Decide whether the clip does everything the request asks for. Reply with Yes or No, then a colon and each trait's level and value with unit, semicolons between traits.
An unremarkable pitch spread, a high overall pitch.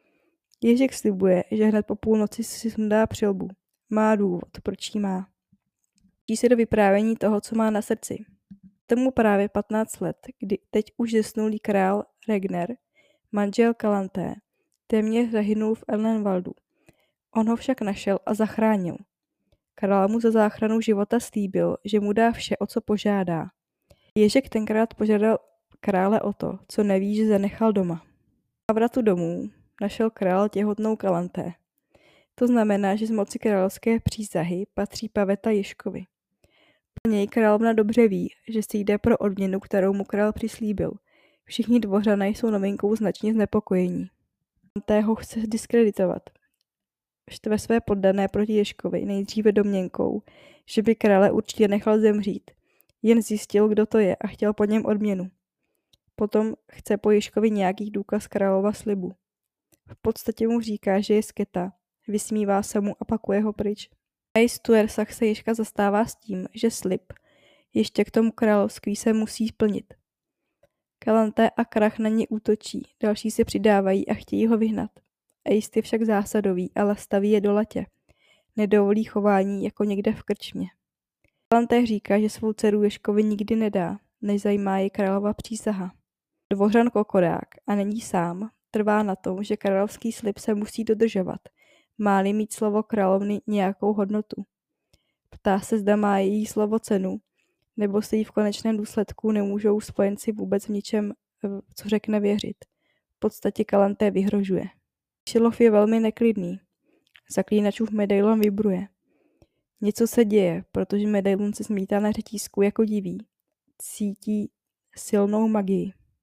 No: narrow, 1.8 semitones; high, 210 Hz